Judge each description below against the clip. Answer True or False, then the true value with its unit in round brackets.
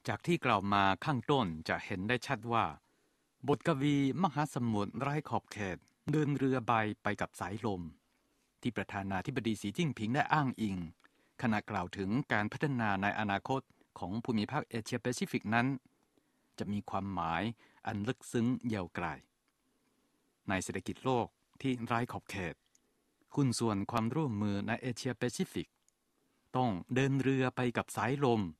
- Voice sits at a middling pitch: False (120 Hz)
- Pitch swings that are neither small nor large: True (4.6 semitones)